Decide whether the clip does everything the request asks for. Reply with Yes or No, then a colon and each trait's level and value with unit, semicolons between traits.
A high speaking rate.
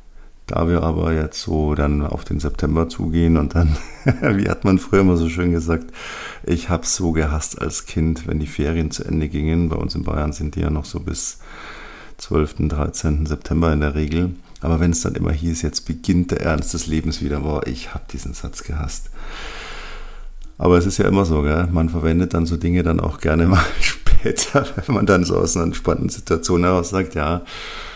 Yes: fast, 205 wpm